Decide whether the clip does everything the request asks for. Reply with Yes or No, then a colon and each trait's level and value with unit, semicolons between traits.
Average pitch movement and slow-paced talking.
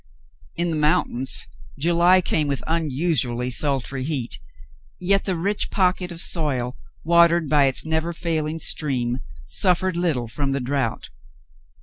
Yes: average, 4.3 semitones; slow, 130 wpm